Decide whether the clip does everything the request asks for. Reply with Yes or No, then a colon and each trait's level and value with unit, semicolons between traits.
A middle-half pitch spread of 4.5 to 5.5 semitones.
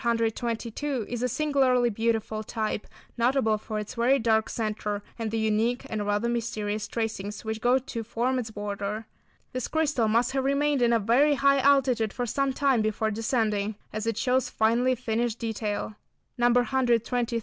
No: narrow, 2.5 semitones